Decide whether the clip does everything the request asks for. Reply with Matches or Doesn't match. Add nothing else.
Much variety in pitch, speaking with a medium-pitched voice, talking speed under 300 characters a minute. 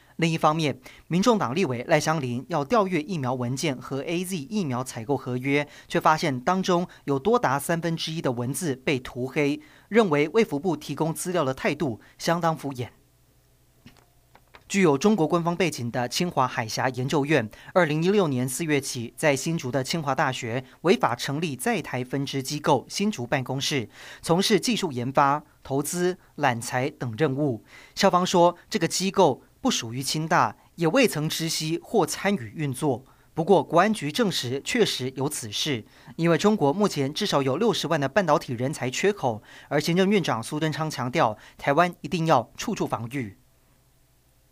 Doesn't match